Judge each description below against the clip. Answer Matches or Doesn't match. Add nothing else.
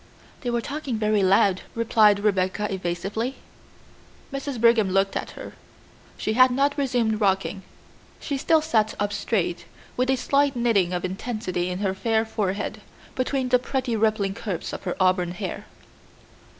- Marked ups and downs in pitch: Doesn't match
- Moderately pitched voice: Doesn't match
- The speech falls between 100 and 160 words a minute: Matches